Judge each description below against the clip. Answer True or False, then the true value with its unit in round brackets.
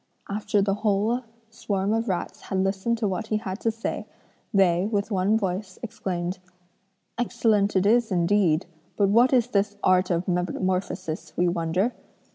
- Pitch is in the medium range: False (200 Hz)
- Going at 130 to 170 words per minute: True (155 wpm)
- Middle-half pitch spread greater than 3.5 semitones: False (2.9 semitones)